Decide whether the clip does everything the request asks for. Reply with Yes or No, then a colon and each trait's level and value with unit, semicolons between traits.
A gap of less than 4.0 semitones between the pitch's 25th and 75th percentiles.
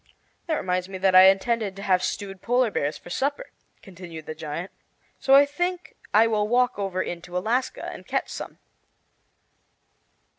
No: average, 5.2 semitones